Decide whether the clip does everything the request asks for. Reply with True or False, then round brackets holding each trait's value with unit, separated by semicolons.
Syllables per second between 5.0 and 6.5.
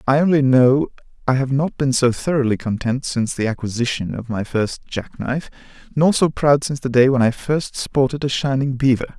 True (5.4 syllables/s)